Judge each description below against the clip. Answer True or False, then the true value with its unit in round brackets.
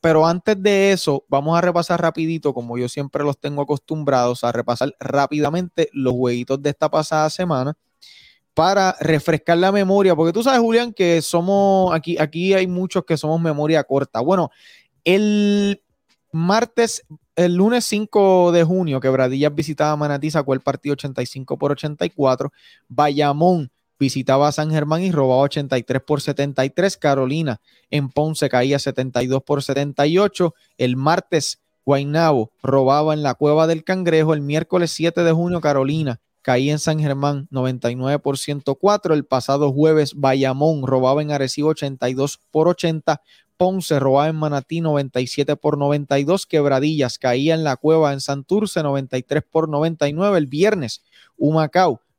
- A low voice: False (150 Hz)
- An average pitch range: True (3.4 semitones)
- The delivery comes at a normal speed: True (145 wpm)